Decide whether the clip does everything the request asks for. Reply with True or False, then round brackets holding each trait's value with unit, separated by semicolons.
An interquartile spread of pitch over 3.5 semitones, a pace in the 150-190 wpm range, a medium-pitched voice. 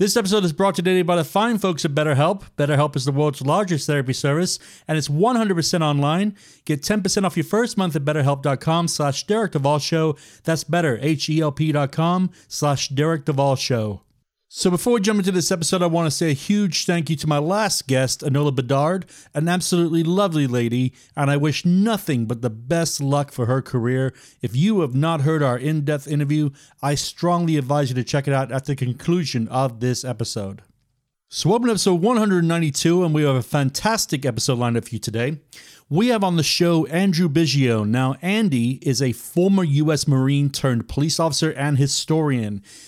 True (4.2 semitones; 180 wpm; 150 Hz)